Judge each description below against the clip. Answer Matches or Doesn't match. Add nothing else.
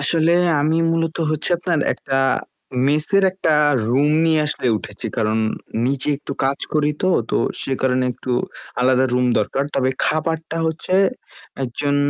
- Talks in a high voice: Doesn't match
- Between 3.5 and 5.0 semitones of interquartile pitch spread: Matches